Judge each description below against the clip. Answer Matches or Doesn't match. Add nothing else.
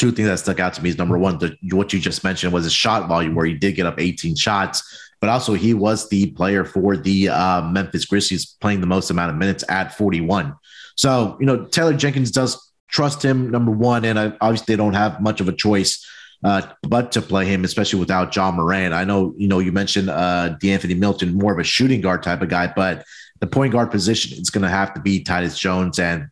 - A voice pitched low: Matches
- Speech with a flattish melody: Doesn't match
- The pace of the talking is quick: Matches